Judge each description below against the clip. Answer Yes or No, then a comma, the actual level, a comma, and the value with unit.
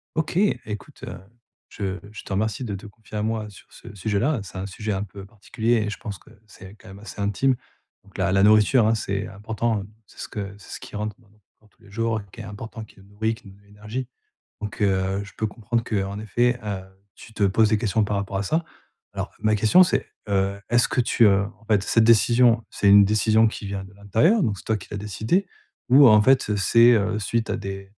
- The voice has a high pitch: No, low, 105 Hz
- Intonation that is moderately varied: No, narrow, 2.1 semitones